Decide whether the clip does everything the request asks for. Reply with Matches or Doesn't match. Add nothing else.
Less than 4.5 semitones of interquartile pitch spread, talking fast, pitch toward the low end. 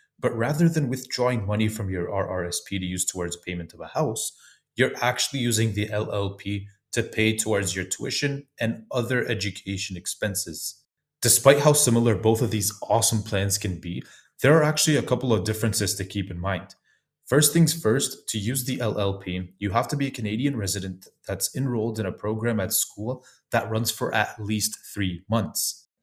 Doesn't match